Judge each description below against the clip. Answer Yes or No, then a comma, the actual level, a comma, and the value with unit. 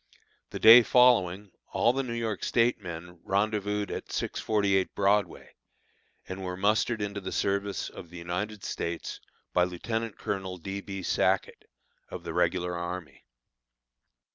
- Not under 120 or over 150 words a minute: Yes, average, 140 wpm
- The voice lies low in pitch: Yes, low, 100 Hz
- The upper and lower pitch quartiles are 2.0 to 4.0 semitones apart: Yes, average, 3.0 semitones